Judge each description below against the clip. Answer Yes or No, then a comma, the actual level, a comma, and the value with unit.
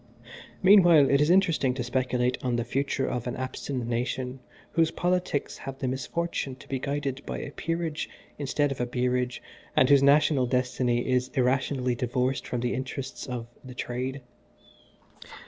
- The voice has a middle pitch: No, low, 130 Hz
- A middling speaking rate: Yes, average, 160 wpm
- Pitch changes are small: Yes, narrow, 2.3 semitones